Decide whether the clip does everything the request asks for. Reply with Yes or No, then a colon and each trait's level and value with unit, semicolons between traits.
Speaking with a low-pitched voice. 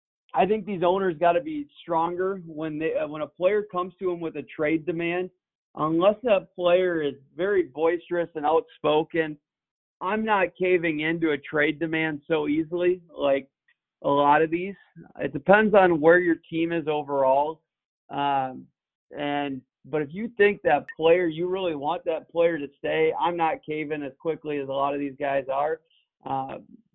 No: medium, 160 Hz